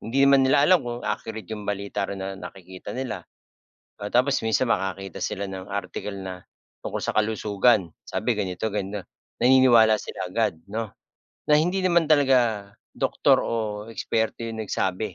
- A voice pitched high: No, low, 110 Hz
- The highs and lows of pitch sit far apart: No, average, 4.3 semitones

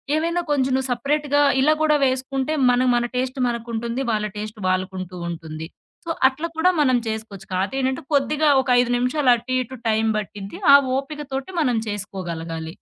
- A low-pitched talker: No, very high, 250 Hz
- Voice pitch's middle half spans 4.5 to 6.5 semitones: Yes, average, 4.8 semitones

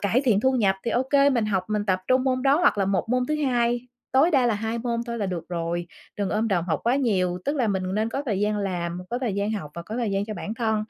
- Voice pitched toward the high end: Yes, high, 220 Hz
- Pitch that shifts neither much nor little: Yes, average, 4.3 semitones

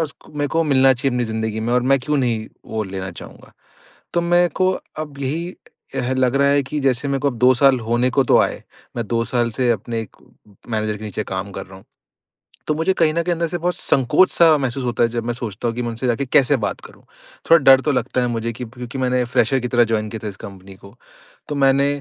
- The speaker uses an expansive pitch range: No, average, 3.6 semitones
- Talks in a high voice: No, low, 125 Hz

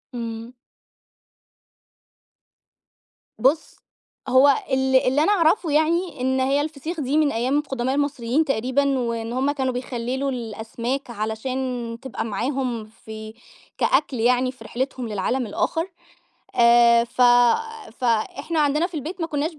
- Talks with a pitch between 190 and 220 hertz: No, very high, 260 Hz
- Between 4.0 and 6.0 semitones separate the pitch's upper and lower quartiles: No, average, 3.6 semitones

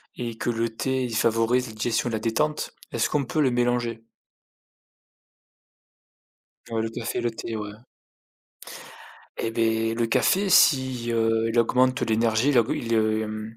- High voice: No, low, 115 Hz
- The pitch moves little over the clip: Yes, narrow, 1.6 semitones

